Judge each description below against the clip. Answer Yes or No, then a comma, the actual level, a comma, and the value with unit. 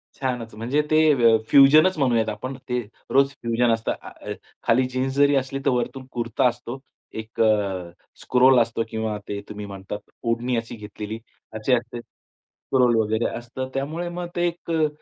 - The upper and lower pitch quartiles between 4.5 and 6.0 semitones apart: No, average, 3.3 semitones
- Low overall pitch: Yes, low, 120 Hz